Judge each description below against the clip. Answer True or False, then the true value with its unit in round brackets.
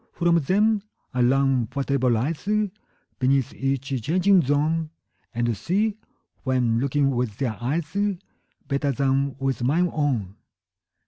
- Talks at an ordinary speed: False (125 wpm)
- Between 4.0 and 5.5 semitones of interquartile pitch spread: True (4.7 semitones)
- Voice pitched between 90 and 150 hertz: True (140 Hz)